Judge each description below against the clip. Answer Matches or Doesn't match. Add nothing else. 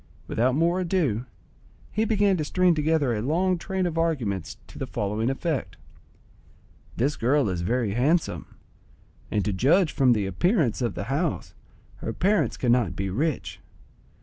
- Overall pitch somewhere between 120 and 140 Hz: Matches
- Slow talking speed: Doesn't match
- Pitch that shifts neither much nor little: Doesn't match